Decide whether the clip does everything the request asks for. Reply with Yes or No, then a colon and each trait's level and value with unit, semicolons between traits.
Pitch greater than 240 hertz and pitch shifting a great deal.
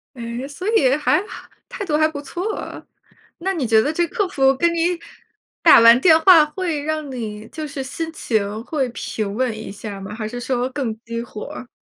Yes: very high, 270 Hz; wide, 5.7 semitones